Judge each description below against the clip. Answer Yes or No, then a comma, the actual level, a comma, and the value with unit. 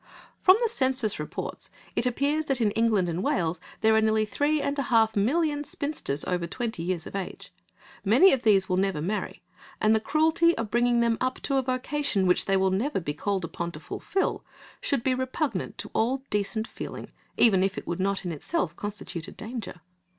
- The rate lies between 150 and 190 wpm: No, average, 200 wpm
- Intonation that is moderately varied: No, wide, 5.8 semitones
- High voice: Yes, high, 220 Hz